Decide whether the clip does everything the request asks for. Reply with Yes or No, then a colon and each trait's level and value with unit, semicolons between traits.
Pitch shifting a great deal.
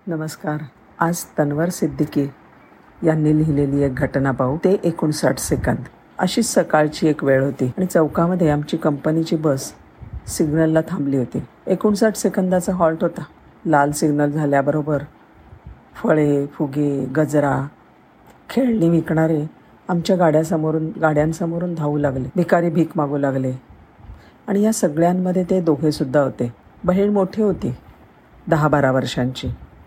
No: average, 3.4 semitones